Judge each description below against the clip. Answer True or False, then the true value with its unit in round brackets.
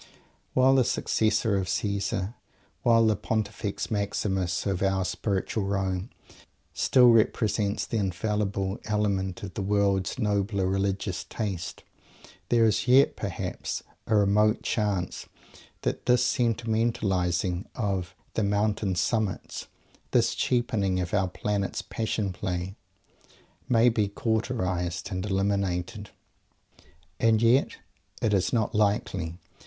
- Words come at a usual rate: False (115 wpm)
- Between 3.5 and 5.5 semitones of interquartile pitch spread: False (2.6 semitones)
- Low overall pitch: True (100 Hz)